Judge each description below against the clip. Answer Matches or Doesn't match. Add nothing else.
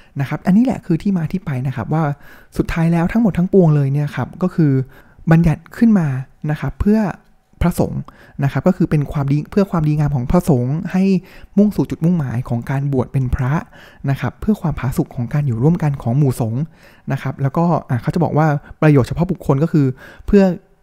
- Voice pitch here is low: Doesn't match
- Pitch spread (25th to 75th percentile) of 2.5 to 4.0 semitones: Doesn't match